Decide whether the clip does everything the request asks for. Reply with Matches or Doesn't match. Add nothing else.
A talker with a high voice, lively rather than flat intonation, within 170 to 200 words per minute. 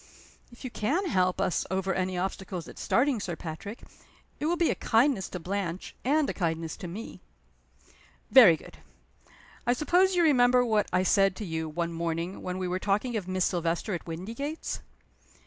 Matches